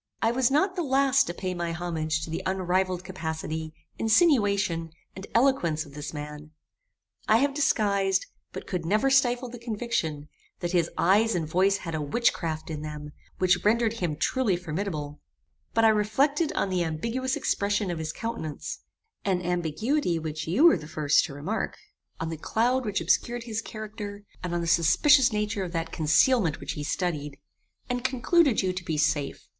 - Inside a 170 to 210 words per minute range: Yes, average, 175 wpm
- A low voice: No, medium, 185 Hz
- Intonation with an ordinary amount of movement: No, wide, 6.4 semitones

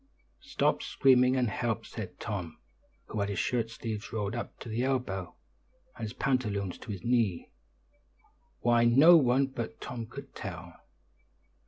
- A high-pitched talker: No, low, 115 Hz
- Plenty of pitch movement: No, average, 3.6 semitones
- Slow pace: No, average, 150 wpm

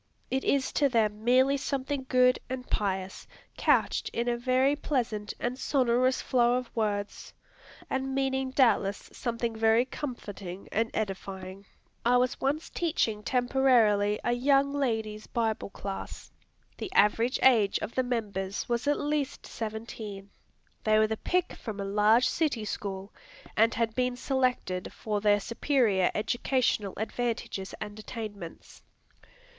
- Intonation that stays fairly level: No, average, 3.7 semitones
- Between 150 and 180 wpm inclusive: No, slow, 135 wpm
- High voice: Yes, high, 235 Hz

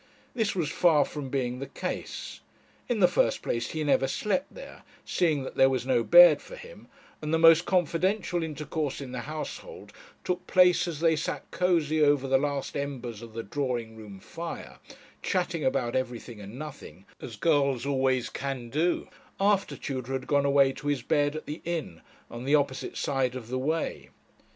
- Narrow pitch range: No, average, 4.3 semitones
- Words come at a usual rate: Yes, average, 180 wpm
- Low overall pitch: No, medium, 145 Hz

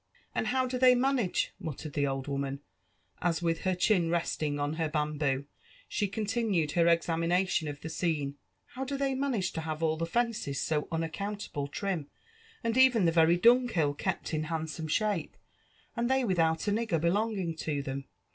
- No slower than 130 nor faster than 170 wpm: No, average, 180 wpm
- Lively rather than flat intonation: Yes, wide, 5.8 semitones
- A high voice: No, medium, 170 Hz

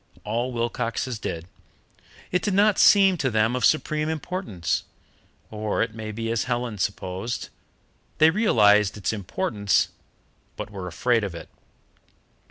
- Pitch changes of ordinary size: No, wide, 6.5 semitones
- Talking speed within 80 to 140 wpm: Yes, slow, 135 wpm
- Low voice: Yes, low, 115 Hz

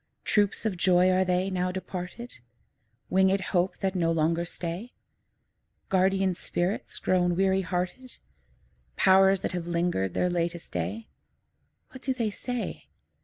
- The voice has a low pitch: No, medium, 185 Hz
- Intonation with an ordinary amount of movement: No, narrow, 1.6 semitones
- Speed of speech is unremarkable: No, slow, 130 wpm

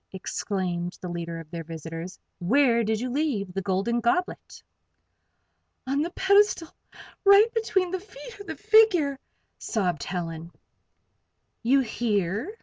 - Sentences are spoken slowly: Yes, slow, 130 wpm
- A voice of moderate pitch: No, high, 235 Hz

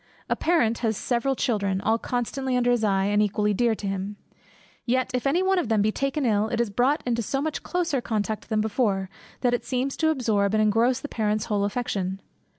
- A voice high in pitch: Yes, high, 230 Hz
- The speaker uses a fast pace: Yes, fast, 215 wpm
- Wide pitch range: No, average, 3.7 semitones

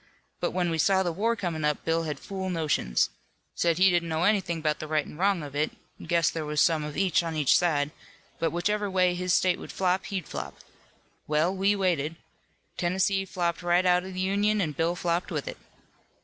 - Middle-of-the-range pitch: Yes, medium, 175 Hz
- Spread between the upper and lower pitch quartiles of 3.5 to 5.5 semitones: No, average, 2.9 semitones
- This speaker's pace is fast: Yes, fast, 210 wpm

